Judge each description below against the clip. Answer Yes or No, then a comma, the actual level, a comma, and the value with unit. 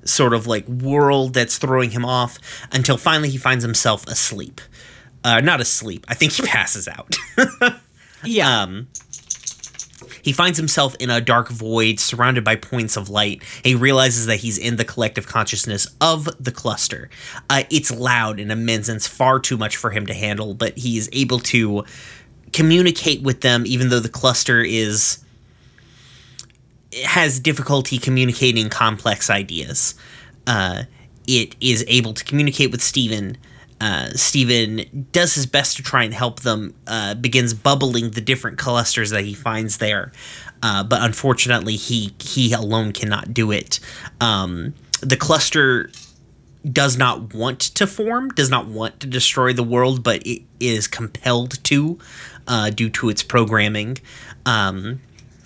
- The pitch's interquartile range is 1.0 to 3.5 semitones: Yes, average, 2.9 semitones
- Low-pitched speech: Yes, low, 120 Hz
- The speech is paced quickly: No, average, 155 wpm